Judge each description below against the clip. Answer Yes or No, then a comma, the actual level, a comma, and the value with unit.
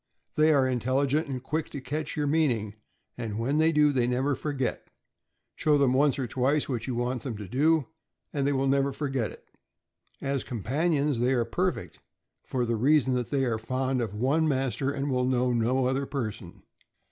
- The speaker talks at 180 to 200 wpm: Yes, average, 195 wpm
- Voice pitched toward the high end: No, low, 135 Hz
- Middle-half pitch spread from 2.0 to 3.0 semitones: Yes, average, 2.7 semitones